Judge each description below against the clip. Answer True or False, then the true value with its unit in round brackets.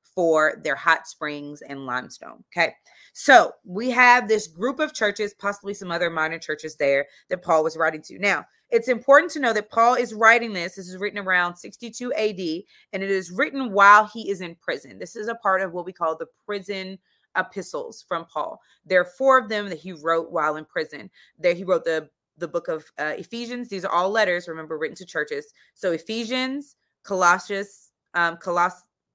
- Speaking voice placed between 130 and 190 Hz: True (185 Hz)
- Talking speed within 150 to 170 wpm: False (200 wpm)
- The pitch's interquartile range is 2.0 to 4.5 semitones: False (5.0 semitones)